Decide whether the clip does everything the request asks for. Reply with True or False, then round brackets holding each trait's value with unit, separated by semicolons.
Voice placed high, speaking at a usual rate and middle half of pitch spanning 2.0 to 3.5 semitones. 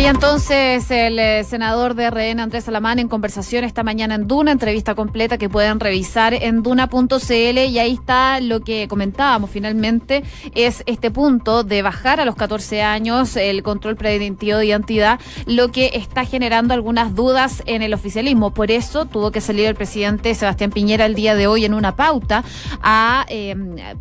True (225 Hz; 170 wpm; 2.5 semitones)